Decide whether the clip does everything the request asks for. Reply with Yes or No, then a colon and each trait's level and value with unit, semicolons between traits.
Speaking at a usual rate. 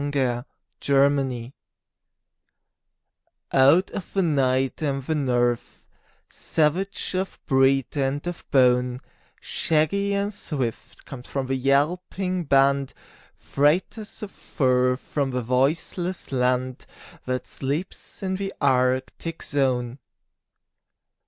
No: slow, 100 wpm